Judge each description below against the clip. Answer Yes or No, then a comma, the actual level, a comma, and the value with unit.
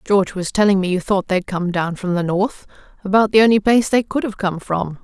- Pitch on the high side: Yes, high, 195 Hz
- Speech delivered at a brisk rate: Yes, fast, 250 wpm